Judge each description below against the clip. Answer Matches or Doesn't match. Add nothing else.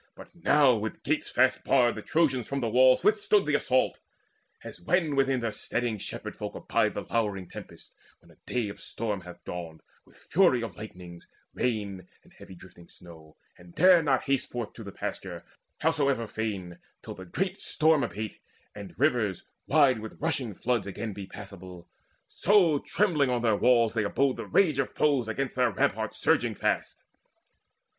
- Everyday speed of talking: Matches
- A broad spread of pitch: Matches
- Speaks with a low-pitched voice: Matches